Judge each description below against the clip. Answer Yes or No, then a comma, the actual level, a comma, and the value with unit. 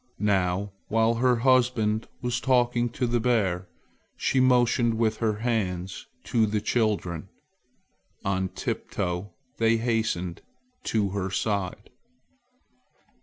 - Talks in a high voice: No, low, 110 Hz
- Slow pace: Yes, slow, 110 wpm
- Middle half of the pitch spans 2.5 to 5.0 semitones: Yes, average, 3.7 semitones